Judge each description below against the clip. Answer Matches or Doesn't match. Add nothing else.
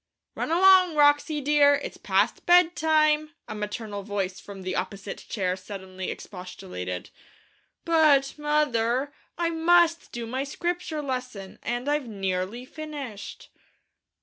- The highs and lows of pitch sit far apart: Matches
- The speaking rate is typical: Doesn't match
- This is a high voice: Matches